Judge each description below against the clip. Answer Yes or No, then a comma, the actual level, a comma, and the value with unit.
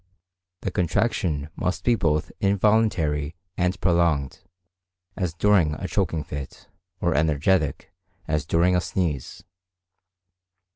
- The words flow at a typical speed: No, slow, 105 wpm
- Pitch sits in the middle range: No, very low, 85 Hz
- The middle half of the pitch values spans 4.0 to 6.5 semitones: No, average, 3.5 semitones